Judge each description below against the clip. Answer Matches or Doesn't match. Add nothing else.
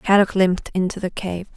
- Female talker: Matches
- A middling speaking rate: Matches